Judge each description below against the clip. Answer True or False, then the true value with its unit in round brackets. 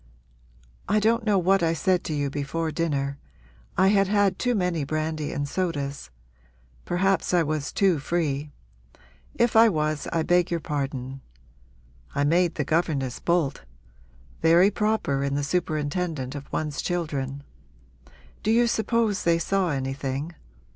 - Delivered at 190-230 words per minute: False (140 wpm)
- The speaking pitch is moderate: True (165 Hz)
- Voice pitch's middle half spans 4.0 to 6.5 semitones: True (4.7 semitones)